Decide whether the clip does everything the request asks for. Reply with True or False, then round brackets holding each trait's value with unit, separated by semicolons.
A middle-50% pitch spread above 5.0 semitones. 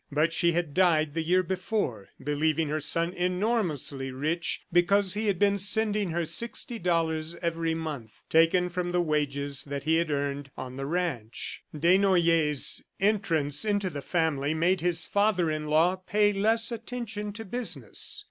False (4.3 semitones)